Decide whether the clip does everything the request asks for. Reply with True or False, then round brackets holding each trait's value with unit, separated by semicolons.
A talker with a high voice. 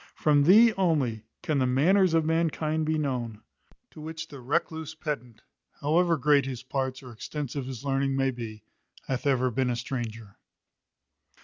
False (140 Hz)